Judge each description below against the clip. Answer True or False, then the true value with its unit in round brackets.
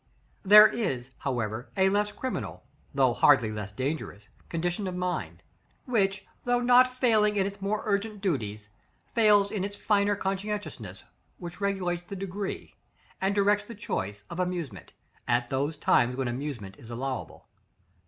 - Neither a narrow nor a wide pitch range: False (7.7 semitones)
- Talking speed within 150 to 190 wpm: True (155 wpm)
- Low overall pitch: False (190 Hz)